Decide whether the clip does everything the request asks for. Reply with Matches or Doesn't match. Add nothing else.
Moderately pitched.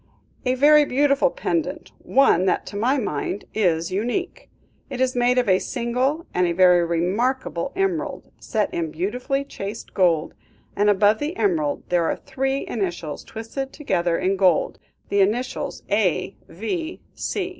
Doesn't match